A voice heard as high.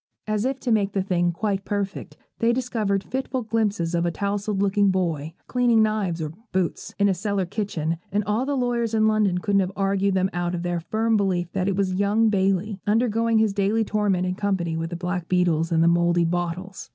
Yes: high, 195 Hz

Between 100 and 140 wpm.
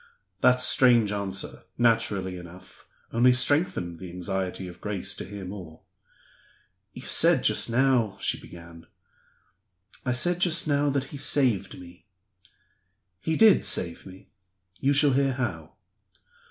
Yes: slow, 135 wpm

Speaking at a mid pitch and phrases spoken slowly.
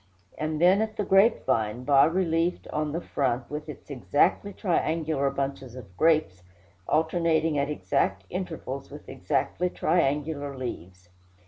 Yes: medium, 150 Hz; slow, 130 wpm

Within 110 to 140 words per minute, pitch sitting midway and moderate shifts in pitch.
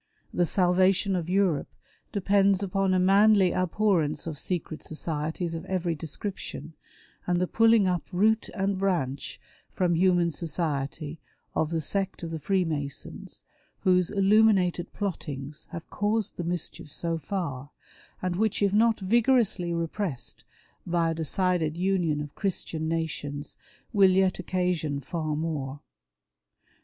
Yes: slow, 135 wpm; medium, 180 Hz; average, 3.4 semitones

